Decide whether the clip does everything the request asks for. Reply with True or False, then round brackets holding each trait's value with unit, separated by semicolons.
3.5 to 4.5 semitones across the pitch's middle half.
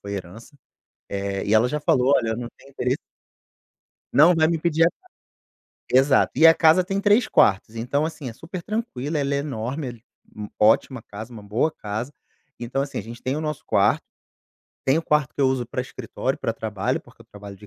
False (5.5 semitones)